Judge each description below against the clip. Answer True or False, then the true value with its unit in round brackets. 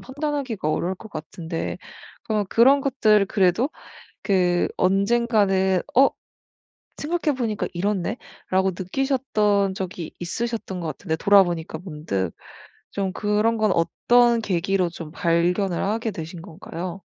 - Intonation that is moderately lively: True (4.5 semitones)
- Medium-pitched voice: False (195 Hz)